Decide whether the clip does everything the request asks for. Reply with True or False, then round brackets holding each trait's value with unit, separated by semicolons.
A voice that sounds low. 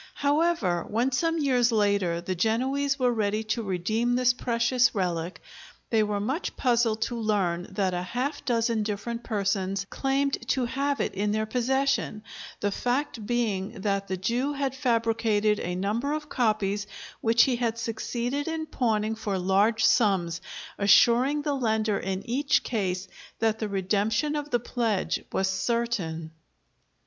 False (225 Hz)